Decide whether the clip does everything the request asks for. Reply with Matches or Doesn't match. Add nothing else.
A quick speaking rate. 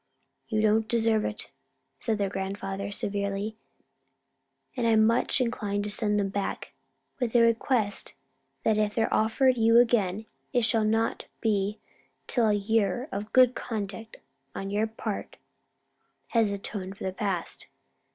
Doesn't match